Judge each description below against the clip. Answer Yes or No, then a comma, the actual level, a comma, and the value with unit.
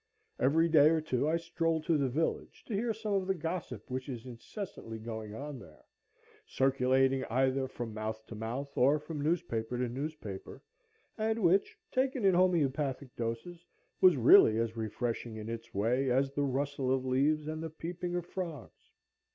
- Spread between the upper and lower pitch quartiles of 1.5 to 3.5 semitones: No, wide, 5.5 semitones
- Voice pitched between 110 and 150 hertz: Yes, low, 135 Hz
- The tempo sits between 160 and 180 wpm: Yes, average, 170 wpm